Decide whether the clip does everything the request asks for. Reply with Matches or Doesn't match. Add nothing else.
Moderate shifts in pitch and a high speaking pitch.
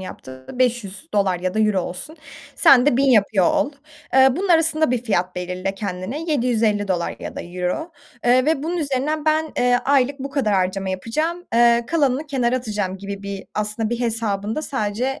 Doesn't match